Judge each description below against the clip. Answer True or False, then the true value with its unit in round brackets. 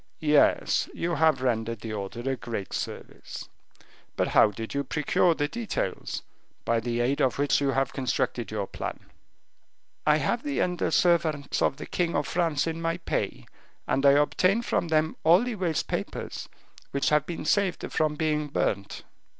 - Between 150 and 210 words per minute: True (170 wpm)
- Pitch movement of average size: True (4.4 semitones)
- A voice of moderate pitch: True (150 Hz)